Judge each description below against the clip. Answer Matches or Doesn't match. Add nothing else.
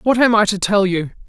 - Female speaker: Matches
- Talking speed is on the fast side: Matches